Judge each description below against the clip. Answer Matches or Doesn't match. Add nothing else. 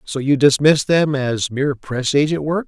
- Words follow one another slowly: Doesn't match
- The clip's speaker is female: Doesn't match